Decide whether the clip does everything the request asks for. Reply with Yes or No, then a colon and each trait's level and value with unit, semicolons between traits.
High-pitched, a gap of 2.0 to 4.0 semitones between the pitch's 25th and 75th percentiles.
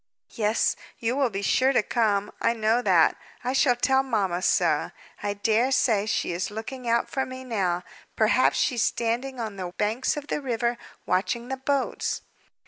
Yes: high, 235 Hz; average, 3.7 semitones